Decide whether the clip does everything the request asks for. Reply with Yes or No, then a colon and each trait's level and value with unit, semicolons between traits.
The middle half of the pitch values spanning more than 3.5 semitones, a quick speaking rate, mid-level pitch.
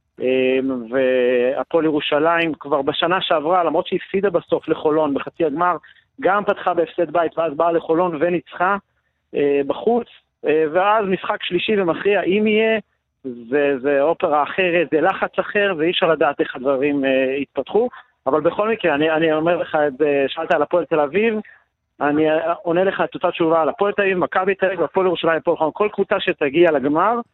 Yes: average, 4.1 semitones; fast, 160 wpm; medium, 170 Hz